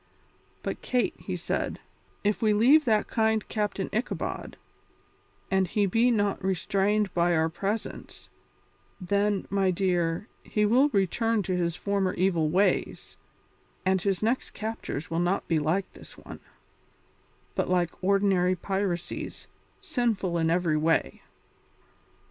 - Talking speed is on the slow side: Yes, slow, 130 wpm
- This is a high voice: Yes, high, 195 Hz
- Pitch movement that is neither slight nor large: Yes, average, 3.2 semitones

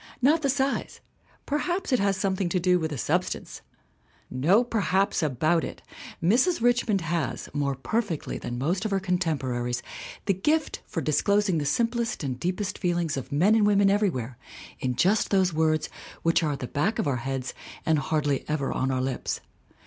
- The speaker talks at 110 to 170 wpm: No, average, 180 wpm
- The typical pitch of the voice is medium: Yes, medium, 175 Hz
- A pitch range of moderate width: No, wide, 6.4 semitones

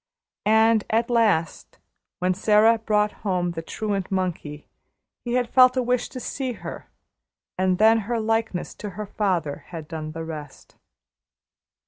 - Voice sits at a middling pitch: No, high, 210 Hz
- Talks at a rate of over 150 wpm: No, average, 145 wpm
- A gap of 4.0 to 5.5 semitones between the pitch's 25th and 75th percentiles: Yes, average, 4.4 semitones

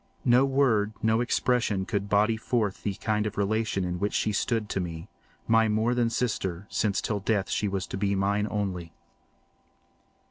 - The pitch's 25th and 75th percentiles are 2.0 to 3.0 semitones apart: Yes, narrow, 2.4 semitones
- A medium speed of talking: Yes, average, 170 wpm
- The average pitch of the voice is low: Yes, low, 105 Hz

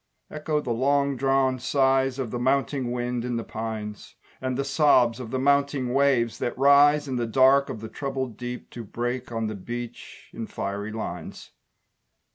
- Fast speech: No, average, 175 wpm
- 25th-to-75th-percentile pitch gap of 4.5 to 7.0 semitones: No, average, 2.7 semitones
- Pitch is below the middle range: Yes, low, 125 Hz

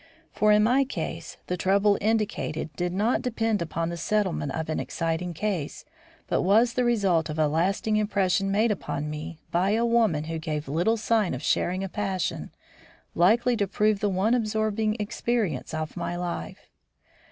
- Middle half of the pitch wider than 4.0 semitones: Yes, average, 4.6 semitones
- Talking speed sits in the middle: Yes, average, 170 wpm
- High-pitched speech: Yes, high, 195 Hz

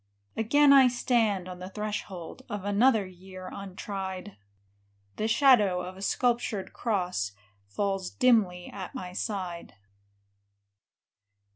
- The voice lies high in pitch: Yes, high, 200 Hz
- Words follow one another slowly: Yes, slow, 110 wpm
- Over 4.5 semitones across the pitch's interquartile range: No, average, 3.4 semitones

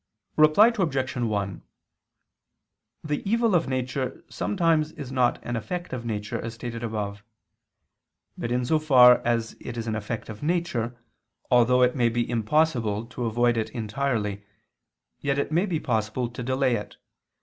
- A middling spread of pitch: Yes, average, 4.3 semitones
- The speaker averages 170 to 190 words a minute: No, average, 155 wpm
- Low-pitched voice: Yes, low, 125 Hz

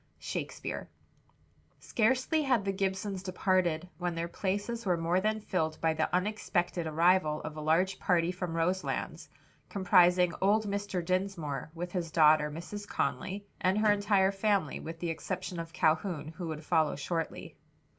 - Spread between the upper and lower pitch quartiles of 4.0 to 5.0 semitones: No, average, 3.2 semitones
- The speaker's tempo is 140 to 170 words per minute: Yes, average, 150 wpm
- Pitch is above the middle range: No, medium, 180 Hz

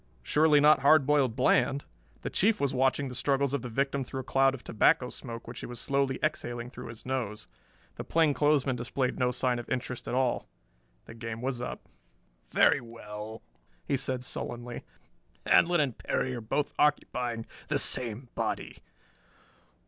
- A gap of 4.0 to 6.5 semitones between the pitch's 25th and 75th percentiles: No, narrow, 2.6 semitones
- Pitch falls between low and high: No, low, 130 Hz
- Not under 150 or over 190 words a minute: Yes, average, 165 wpm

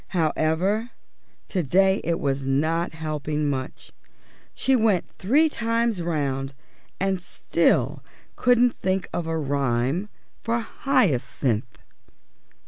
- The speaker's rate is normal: No, slow, 105 wpm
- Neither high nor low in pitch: Yes, medium, 170 Hz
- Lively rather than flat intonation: Yes, wide, 6.8 semitones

